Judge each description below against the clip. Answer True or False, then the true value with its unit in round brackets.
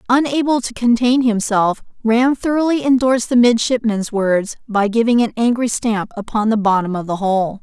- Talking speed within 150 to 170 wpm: True (165 wpm)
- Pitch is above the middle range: True (230 Hz)